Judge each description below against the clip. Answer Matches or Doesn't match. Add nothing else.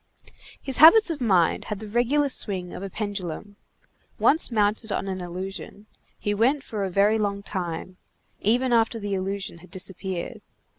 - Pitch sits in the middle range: Doesn't match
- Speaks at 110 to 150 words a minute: Doesn't match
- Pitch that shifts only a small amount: Doesn't match